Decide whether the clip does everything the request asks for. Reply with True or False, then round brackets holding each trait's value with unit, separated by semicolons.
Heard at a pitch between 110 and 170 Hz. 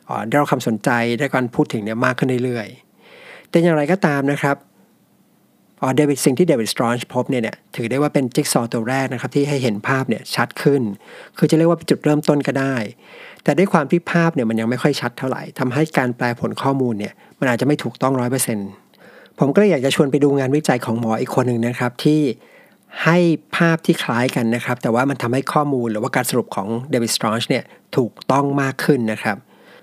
True (135 Hz)